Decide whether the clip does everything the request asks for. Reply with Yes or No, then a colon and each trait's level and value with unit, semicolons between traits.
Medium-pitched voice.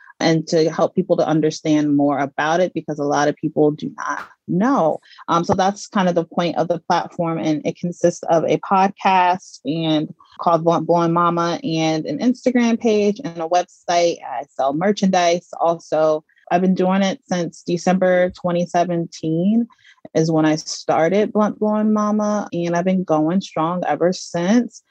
Yes: medium, 175 Hz